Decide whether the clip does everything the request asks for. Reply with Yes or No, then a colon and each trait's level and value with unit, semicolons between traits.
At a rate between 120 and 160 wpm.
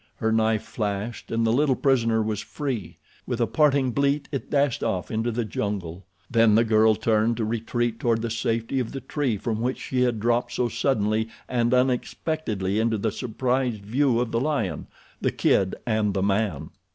No: average, 185 wpm